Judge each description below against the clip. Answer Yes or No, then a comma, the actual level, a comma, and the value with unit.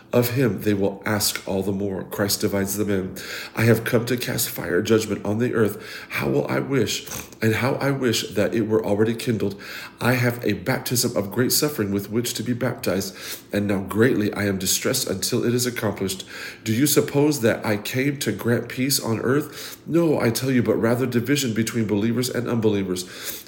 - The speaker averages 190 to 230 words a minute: Yes, average, 200 wpm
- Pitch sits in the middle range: No, low, 115 Hz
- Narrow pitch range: No, average, 3.2 semitones